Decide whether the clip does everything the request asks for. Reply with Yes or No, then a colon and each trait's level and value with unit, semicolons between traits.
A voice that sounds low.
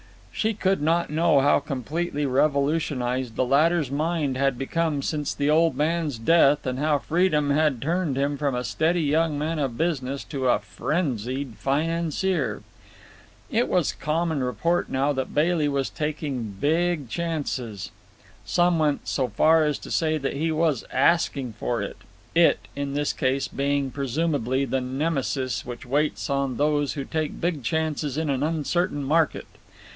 No: medium, 145 Hz